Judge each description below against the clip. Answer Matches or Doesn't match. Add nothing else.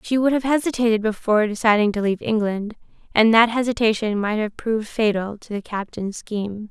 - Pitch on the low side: Doesn't match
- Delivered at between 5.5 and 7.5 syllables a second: Matches